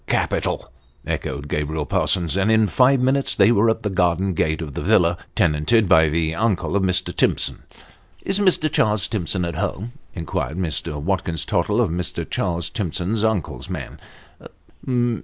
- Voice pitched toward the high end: No, very low, 90 Hz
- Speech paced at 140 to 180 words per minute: Yes, average, 175 wpm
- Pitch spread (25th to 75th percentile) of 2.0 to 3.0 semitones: No, average, 5.1 semitones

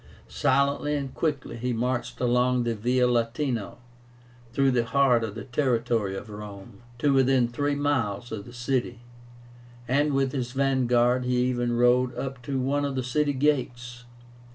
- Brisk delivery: No, average, 155 wpm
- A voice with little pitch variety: Yes, narrow, 2.3 semitones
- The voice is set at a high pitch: No, low, 125 Hz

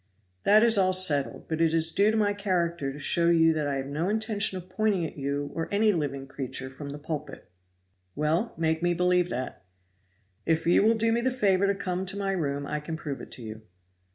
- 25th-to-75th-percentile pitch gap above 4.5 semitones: Yes, average, 5.3 semitones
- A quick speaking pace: Yes, fast, 225 wpm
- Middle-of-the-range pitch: Yes, medium, 170 Hz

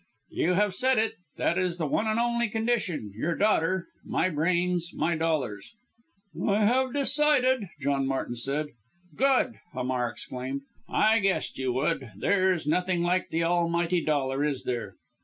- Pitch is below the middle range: No, medium, 175 Hz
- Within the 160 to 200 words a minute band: No, average, 150 wpm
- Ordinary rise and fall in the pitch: No, wide, 7.5 semitones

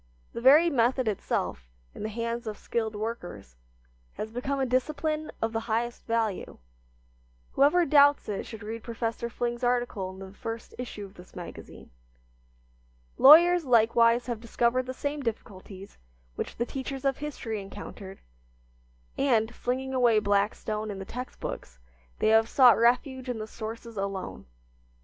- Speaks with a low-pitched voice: No, high, 230 Hz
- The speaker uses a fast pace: No, average, 150 wpm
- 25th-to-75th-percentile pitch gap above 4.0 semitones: No, average, 3.2 semitones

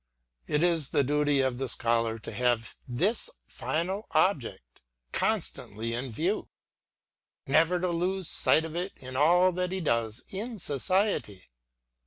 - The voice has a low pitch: No, medium, 150 Hz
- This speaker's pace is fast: No, average, 145 wpm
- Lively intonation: Yes, wide, 7.1 semitones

